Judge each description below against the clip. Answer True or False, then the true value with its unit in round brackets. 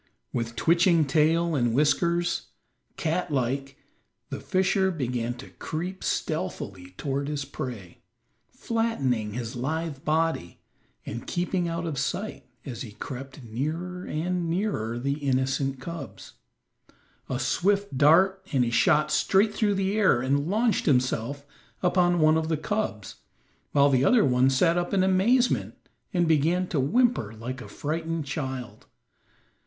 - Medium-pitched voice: True (150 Hz)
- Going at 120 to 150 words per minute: True (140 wpm)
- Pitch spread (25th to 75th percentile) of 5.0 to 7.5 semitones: True (5.4 semitones)